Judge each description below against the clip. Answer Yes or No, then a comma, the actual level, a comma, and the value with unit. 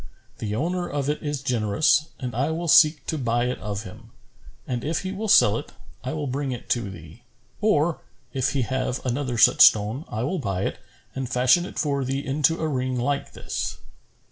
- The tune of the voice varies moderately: Yes, average, 4.0 semitones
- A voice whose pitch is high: No, low, 135 Hz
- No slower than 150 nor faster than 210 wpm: Yes, average, 200 wpm